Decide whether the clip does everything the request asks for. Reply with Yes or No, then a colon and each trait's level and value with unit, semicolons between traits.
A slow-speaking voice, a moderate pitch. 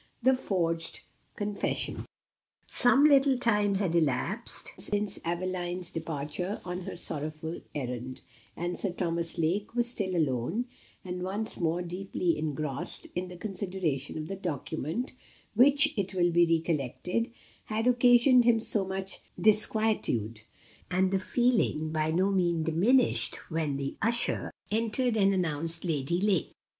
Yes: slow, 130 wpm; medium, 180 Hz